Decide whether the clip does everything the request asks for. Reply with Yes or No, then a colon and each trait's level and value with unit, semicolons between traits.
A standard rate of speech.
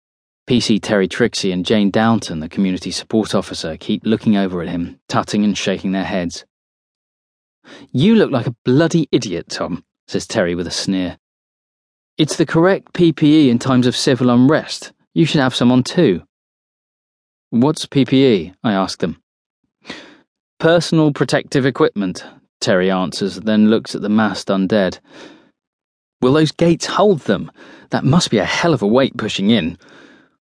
Yes: average, 155 wpm